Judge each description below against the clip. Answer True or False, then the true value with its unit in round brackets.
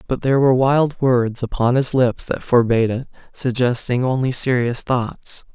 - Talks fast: False (150 wpm)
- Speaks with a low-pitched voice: True (125 Hz)